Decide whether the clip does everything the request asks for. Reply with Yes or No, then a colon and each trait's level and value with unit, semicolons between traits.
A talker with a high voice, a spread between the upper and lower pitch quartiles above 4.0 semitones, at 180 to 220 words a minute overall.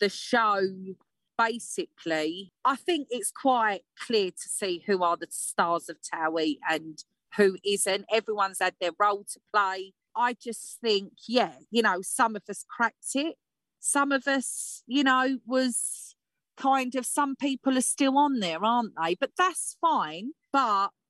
No: high, 220 Hz; wide, 5.5 semitones; average, 160 wpm